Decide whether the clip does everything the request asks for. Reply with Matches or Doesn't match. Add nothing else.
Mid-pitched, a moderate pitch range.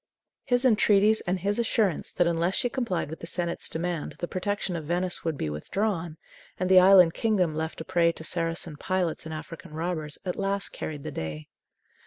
Matches